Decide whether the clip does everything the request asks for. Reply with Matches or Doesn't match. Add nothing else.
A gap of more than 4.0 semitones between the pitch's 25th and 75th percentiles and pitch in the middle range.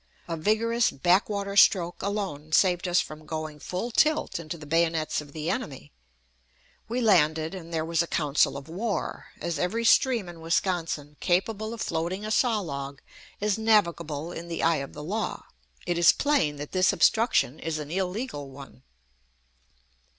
Matches